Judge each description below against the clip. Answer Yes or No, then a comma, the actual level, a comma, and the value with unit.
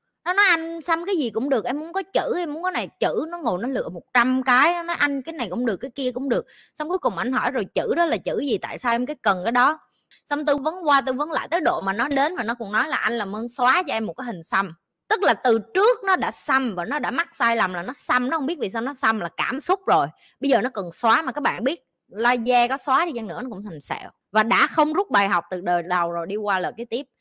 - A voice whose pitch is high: Yes, very high, 255 Hz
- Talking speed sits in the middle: No, fast, 310 wpm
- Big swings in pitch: Yes, wide, 5.8 semitones